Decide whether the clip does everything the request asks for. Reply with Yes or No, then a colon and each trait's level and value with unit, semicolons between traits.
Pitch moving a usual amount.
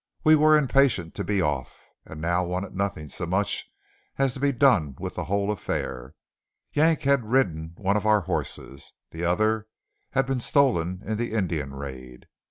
No: wide, 7.9 semitones